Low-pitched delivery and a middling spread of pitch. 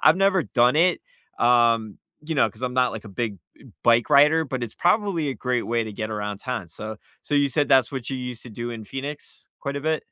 Yes: low, 125 Hz; average, 4.2 semitones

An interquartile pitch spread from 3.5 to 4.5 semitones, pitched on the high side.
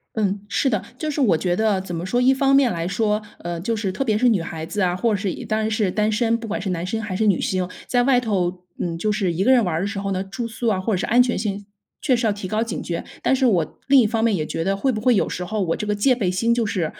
Yes: average, 3.9 semitones; high, 210 Hz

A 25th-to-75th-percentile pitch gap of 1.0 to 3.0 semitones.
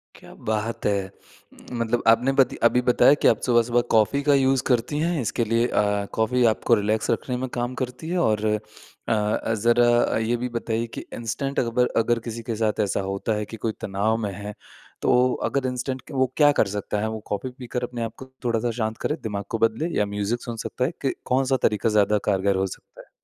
Yes: average, 2.7 semitones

